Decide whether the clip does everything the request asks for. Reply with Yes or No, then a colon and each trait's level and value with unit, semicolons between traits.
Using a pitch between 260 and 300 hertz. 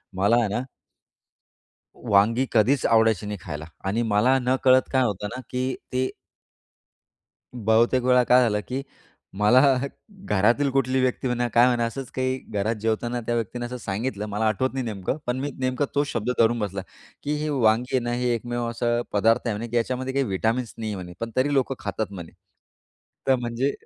No: low, 120 Hz